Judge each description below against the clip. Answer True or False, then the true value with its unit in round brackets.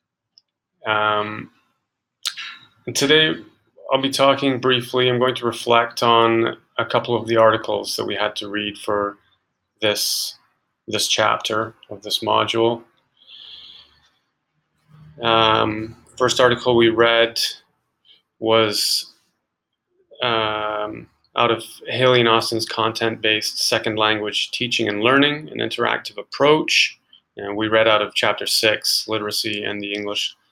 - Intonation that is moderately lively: False (2.3 semitones)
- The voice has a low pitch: True (115 Hz)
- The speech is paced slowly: True (120 wpm)